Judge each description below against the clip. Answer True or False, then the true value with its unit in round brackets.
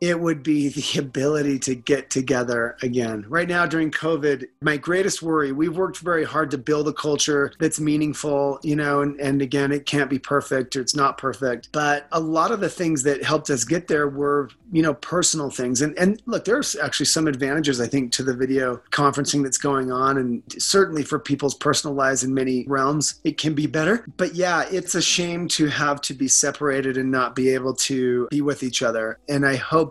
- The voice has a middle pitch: True (145 Hz)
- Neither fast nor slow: False (215 wpm)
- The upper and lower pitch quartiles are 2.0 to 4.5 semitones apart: True (2.6 semitones)